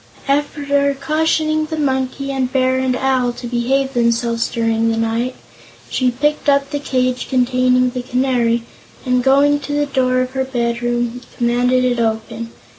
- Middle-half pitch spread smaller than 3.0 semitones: Yes, narrow, 2.4 semitones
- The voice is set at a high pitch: Yes, very high, 255 Hz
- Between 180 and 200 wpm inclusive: No, average, 160 wpm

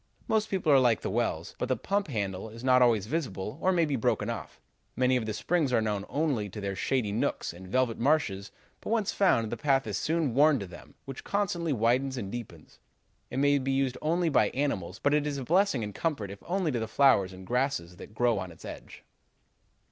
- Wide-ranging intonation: Yes, wide, 5.8 semitones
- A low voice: Yes, low, 125 Hz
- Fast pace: Yes, fast, 225 wpm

